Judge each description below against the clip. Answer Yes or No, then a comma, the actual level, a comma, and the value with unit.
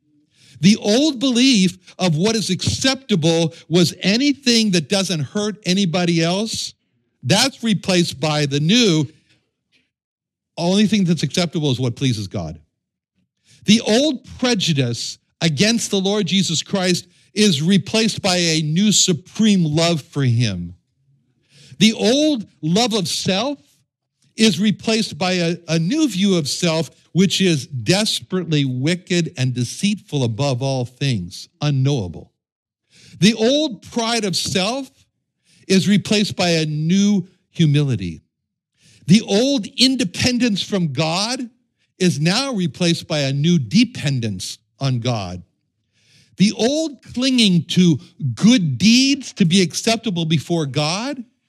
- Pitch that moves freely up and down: Yes, wide, 6.3 semitones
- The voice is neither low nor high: Yes, medium, 175 Hz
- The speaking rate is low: Yes, slow, 120 wpm